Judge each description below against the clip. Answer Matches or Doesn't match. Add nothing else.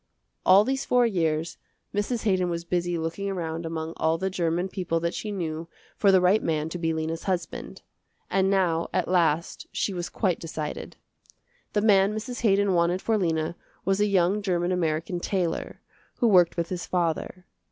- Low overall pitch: Doesn't match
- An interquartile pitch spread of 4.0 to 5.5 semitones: Doesn't match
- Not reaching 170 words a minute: Doesn't match